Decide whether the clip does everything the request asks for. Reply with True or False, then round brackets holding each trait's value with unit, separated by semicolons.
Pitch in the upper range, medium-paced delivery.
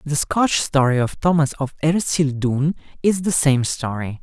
False (145 Hz; 155 wpm)